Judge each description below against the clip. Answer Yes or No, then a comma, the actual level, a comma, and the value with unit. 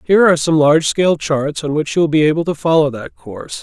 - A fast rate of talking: Yes, fast, 250 wpm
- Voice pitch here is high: No, medium, 155 Hz